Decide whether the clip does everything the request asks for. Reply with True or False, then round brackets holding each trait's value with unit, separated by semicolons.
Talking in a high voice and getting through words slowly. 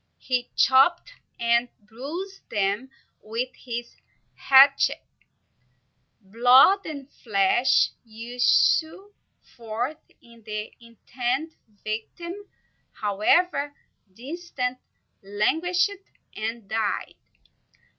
True (245 Hz; 75 wpm)